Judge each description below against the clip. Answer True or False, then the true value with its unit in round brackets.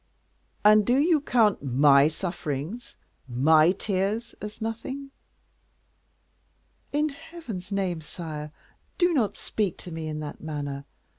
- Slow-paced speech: True (120 wpm)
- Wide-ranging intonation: True (7.6 semitones)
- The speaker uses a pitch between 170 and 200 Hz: True (190 Hz)